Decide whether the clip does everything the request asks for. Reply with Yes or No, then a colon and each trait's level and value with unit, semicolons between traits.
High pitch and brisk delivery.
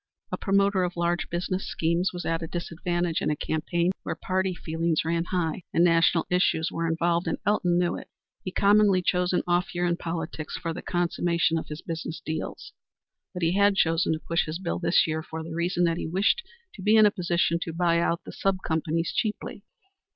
No: medium, 170 Hz; fast, 210 wpm